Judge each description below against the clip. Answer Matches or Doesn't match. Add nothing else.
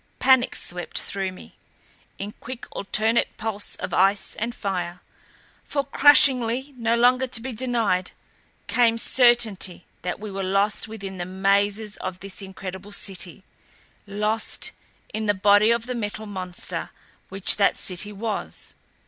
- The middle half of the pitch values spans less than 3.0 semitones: Doesn't match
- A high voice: Matches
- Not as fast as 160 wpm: Matches